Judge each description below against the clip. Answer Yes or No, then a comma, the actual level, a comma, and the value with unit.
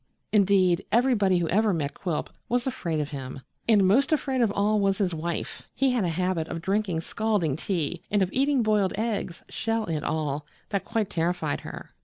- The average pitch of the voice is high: Yes, high, 195 Hz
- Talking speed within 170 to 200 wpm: Yes, average, 190 wpm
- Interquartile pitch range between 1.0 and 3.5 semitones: No, average, 4.7 semitones